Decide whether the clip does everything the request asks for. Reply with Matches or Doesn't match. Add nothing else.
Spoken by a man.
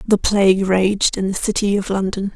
Doesn't match